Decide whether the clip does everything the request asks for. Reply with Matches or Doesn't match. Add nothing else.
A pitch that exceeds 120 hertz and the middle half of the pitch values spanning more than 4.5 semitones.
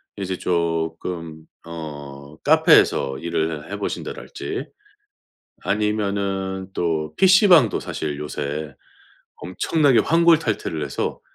Doesn't match